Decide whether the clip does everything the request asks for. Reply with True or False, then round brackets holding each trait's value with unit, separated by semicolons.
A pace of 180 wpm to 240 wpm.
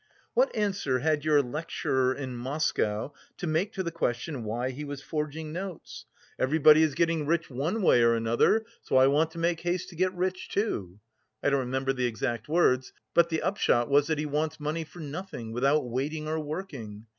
True (190 wpm)